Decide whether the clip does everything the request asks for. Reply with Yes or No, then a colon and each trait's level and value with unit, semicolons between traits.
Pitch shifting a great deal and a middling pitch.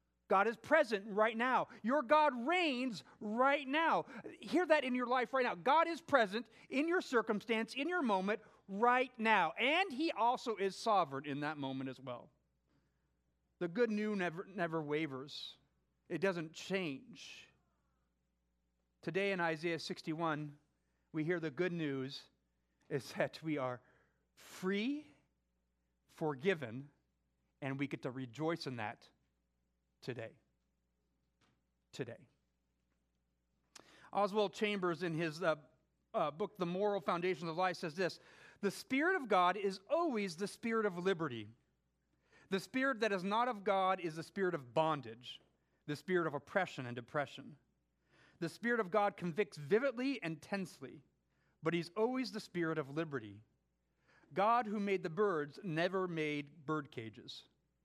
Yes: wide, 8.3 semitones; medium, 170 Hz